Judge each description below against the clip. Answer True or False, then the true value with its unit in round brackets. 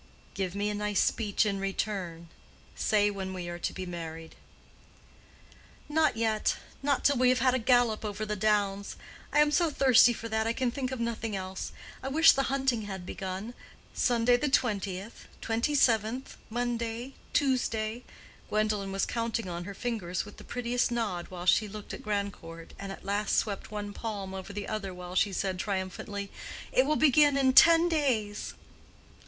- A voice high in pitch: True (215 Hz)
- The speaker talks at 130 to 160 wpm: False (175 wpm)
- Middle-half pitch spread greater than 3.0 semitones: True (4.0 semitones)